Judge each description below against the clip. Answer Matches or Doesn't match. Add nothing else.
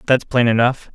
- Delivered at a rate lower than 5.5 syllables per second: Matches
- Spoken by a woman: Doesn't match